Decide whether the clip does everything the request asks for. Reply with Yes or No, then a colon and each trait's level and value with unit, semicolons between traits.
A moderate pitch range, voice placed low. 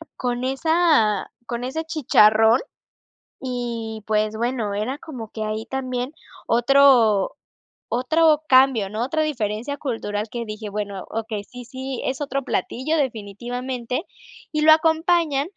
No: average, 4.2 semitones; high, 245 Hz